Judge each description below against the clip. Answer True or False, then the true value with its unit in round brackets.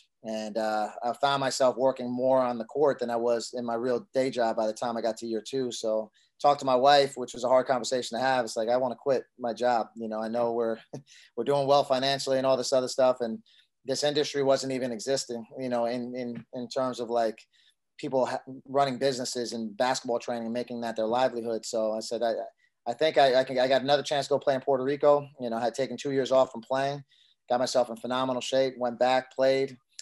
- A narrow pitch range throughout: True (2.3 semitones)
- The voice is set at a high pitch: False (125 Hz)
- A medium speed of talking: False (245 wpm)